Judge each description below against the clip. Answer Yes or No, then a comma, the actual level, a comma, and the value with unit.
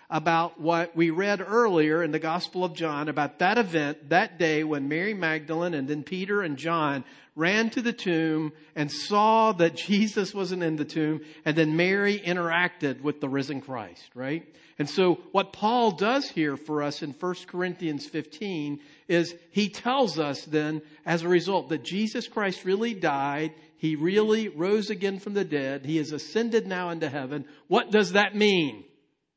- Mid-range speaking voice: Yes, medium, 170 Hz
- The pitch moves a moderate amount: Yes, average, 4.5 semitones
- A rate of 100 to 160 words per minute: No, average, 175 wpm